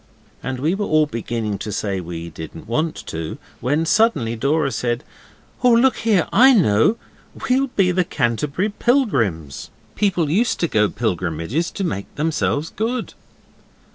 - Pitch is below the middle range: No, medium, 150 Hz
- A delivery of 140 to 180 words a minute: Yes, average, 145 wpm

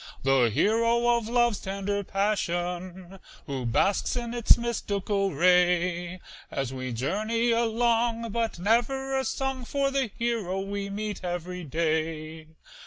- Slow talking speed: Yes, slow, 125 wpm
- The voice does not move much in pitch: No, average, 5.0 semitones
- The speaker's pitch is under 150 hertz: No, high, 200 Hz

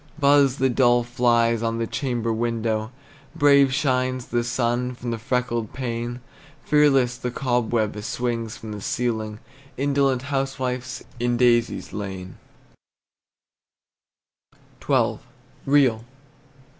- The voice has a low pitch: Yes, low, 120 Hz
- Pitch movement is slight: Yes, narrow, 2.1 semitones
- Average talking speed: No, slow, 105 wpm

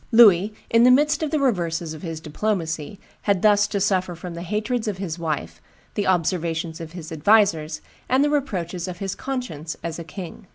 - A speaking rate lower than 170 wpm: No, average, 195 wpm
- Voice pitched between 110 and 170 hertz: No, medium, 185 Hz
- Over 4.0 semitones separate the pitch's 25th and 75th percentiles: Yes, average, 4.6 semitones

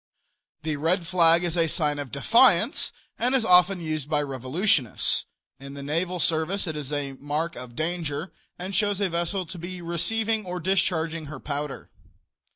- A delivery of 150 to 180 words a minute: Yes, average, 165 wpm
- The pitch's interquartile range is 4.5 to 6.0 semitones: No, average, 3.7 semitones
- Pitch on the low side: No, medium, 165 Hz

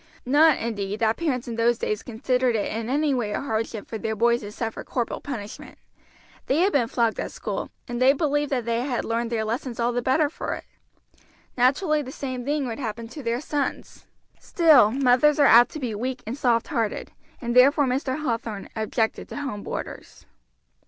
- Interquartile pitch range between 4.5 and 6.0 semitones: No, average, 3.4 semitones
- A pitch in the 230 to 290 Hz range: Yes, high, 245 Hz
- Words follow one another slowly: No, average, 195 wpm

